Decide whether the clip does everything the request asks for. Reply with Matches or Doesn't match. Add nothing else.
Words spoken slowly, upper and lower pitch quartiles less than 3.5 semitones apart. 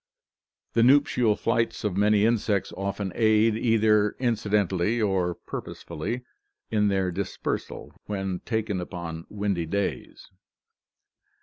Matches